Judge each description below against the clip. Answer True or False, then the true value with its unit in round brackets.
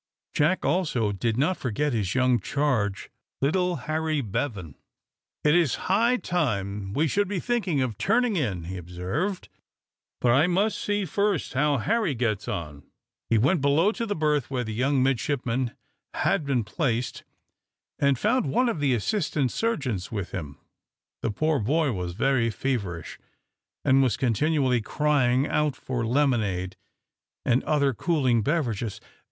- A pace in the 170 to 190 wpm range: False (145 wpm)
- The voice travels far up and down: True (6.0 semitones)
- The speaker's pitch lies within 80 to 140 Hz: True (135 Hz)